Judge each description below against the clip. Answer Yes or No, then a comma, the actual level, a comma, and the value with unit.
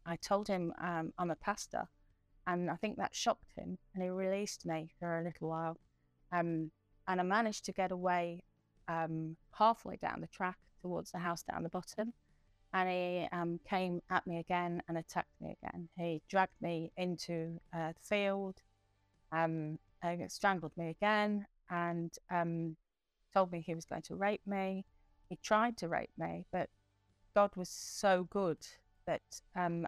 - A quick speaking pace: No, average, 170 wpm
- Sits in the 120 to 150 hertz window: No, medium, 175 Hz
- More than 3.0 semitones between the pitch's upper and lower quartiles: No, narrow, 2.5 semitones